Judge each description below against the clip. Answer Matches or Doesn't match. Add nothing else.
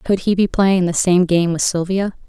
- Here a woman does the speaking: Matches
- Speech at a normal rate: Doesn't match